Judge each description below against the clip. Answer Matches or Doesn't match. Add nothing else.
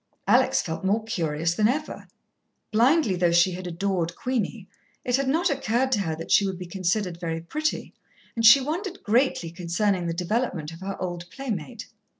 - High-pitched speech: Matches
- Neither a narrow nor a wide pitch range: Doesn't match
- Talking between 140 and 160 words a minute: Doesn't match